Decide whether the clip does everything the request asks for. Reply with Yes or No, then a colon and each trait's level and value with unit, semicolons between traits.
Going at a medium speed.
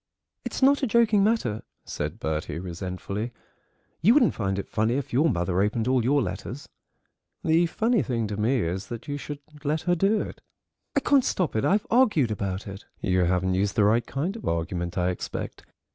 Yes: average, 190 wpm